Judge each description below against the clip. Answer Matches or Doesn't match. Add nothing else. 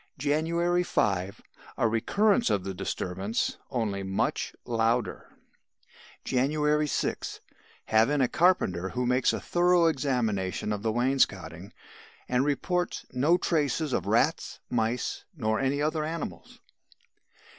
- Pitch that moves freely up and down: Matches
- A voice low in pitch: Matches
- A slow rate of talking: Matches